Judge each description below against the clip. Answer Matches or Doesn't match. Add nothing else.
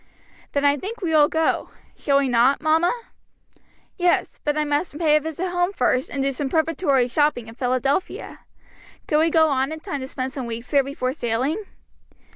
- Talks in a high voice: Matches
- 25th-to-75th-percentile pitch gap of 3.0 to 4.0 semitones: Matches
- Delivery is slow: Doesn't match